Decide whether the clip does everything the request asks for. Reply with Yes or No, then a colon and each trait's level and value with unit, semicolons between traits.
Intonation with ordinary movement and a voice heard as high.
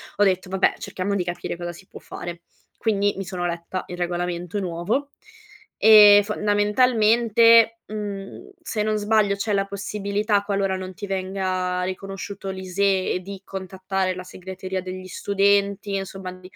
No: narrow, 1.8 semitones; high, 195 Hz